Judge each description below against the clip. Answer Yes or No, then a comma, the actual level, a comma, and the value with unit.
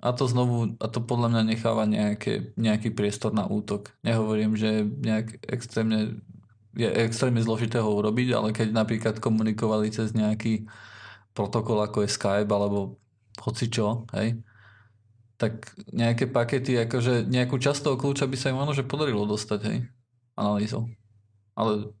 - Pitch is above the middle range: No, low, 110 Hz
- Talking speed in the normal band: Yes, average, 145 wpm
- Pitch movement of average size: No, narrow, 2.0 semitones